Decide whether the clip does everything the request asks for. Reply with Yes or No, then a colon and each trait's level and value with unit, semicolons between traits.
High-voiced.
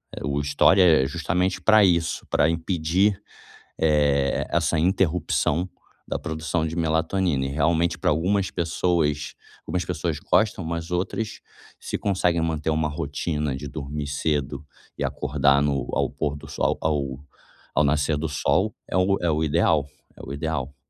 No: very low, 80 Hz